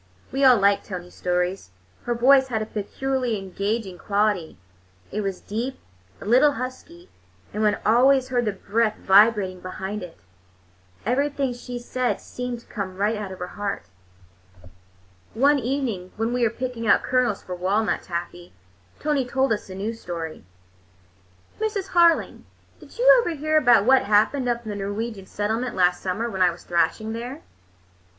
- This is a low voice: No, high, 225 Hz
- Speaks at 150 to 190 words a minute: Yes, average, 160 wpm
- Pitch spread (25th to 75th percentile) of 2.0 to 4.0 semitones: No, average, 4.6 semitones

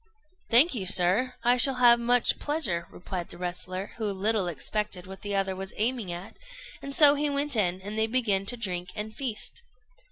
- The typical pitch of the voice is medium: No, high, 215 Hz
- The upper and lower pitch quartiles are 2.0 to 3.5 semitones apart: No, average, 4.7 semitones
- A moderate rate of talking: Yes, average, 195 wpm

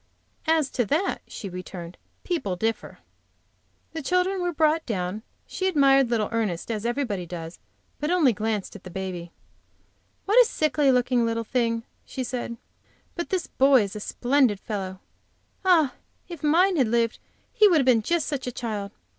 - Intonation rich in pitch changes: Yes, wide, 6.8 semitones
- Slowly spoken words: No, average, 165 wpm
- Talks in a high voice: Yes, high, 245 Hz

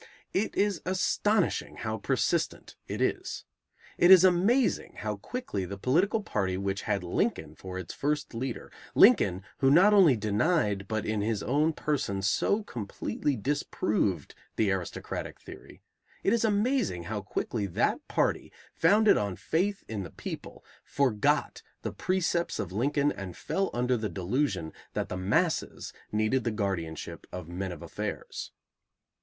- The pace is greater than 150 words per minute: No, average, 145 wpm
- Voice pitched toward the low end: Yes, low, 115 Hz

